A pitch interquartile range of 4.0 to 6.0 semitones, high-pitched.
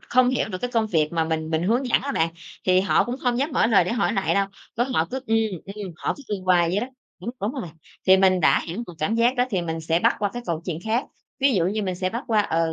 Yes: wide, 5.5 semitones; high, 200 Hz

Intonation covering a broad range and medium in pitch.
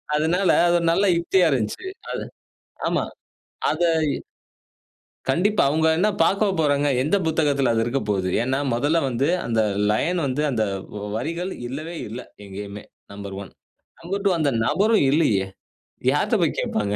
Yes: wide, 7.0 semitones; medium, 145 Hz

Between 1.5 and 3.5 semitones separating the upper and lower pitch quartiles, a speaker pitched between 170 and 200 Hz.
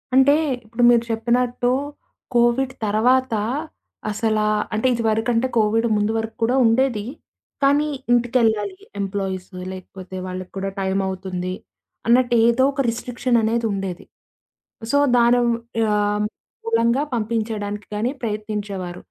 No: average, 2.8 semitones; high, 225 Hz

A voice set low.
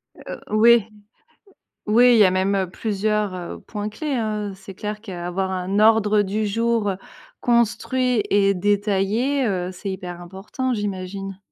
No: high, 205 Hz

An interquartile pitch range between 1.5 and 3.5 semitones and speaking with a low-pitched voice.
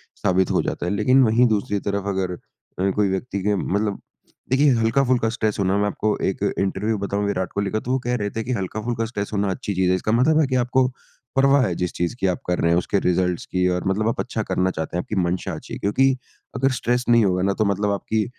No: average, 4.0 semitones; low, 105 Hz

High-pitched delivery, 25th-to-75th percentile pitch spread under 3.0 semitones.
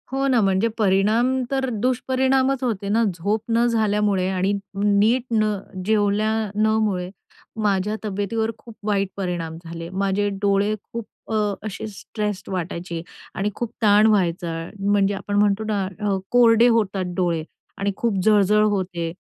Yes: high, 205 Hz; narrow, 2.5 semitones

